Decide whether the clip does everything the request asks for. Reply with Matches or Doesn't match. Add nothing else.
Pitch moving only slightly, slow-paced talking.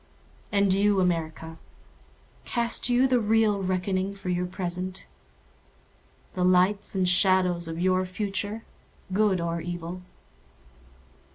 Matches